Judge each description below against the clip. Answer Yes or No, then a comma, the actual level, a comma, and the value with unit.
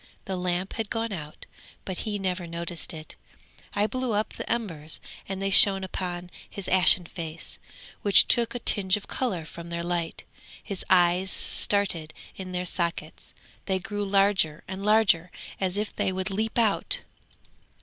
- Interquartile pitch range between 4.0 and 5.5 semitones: No, average, 2.8 semitones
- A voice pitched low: No, high, 190 Hz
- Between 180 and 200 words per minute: No, average, 160 wpm